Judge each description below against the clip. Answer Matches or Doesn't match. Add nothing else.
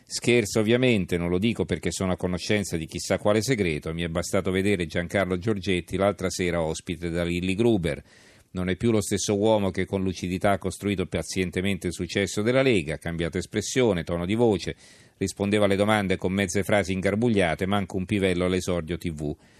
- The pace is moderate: Doesn't match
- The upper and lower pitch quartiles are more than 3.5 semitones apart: Doesn't match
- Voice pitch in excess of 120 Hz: Doesn't match